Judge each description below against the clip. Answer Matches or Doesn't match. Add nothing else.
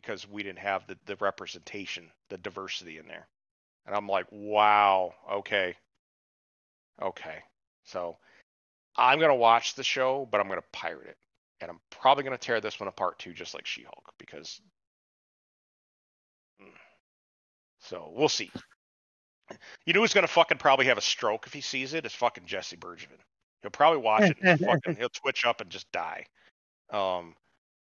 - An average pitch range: Doesn't match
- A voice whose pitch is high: Doesn't match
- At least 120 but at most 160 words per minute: Doesn't match